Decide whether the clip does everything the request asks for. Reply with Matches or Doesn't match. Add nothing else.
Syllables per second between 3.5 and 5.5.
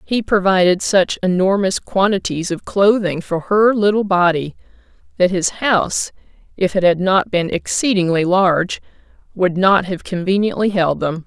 Matches